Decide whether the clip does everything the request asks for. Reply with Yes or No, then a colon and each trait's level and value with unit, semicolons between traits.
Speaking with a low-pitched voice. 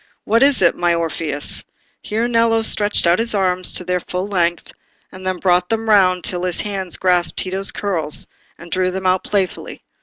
No: medium, 185 Hz